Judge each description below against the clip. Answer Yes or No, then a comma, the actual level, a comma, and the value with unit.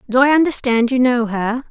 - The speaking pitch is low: No, very high, 250 Hz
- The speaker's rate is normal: No, fast, 210 wpm